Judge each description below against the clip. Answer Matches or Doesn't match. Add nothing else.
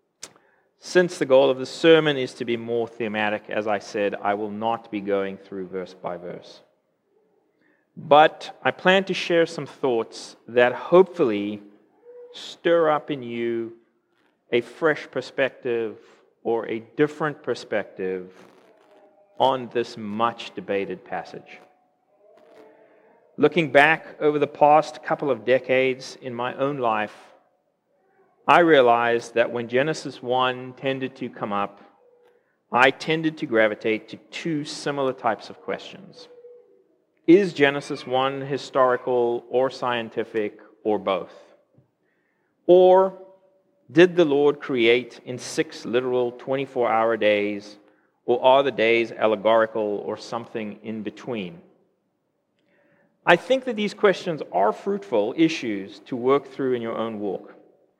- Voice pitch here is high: Doesn't match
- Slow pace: Matches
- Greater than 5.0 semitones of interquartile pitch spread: Matches